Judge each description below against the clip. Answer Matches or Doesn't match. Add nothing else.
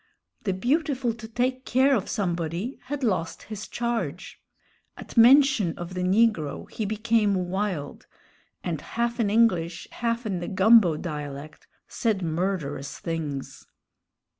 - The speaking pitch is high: Matches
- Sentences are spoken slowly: Matches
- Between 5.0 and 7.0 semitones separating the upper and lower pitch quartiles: Matches